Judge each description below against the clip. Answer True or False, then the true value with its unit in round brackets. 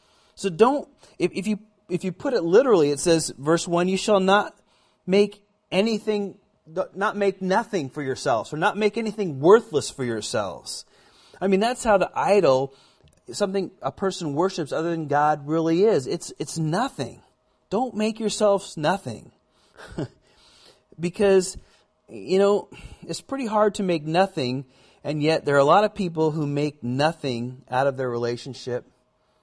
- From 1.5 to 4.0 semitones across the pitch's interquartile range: False (5.5 semitones)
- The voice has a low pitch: False (180 Hz)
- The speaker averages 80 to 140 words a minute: False (155 wpm)